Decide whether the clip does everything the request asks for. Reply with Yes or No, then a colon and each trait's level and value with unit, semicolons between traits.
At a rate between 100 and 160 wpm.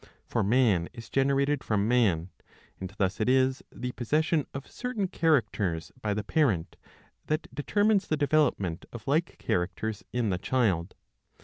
Yes: average, 145 wpm